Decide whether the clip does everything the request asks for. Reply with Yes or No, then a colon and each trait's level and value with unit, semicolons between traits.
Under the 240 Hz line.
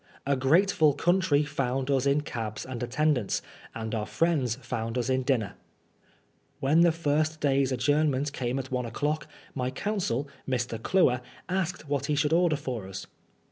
Yes: medium, 140 Hz